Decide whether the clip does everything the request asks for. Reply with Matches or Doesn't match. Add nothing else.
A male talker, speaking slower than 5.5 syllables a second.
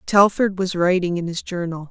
Doesn't match